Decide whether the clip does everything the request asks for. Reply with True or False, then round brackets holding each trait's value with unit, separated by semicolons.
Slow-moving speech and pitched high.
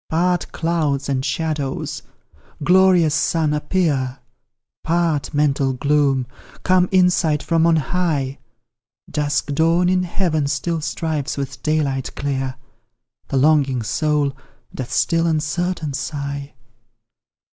False (105 wpm; 150 Hz)